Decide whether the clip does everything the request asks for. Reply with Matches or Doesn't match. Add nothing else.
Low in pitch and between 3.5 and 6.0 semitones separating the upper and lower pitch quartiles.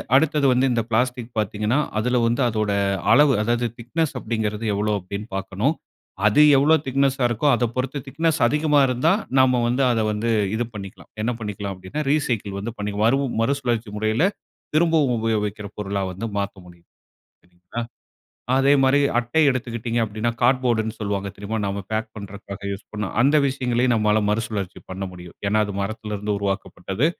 Matches